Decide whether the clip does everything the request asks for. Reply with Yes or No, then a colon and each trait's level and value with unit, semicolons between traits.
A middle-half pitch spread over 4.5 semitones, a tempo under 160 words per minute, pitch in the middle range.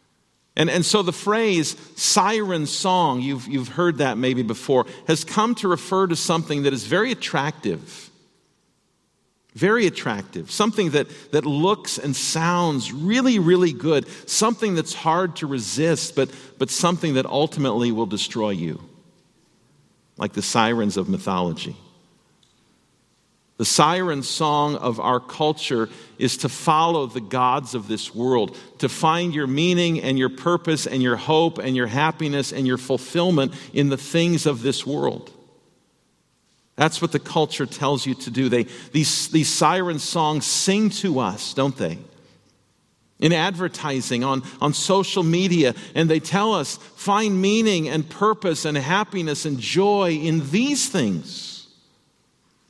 Yes: average, 4.9 semitones; average, 145 wpm; medium, 155 Hz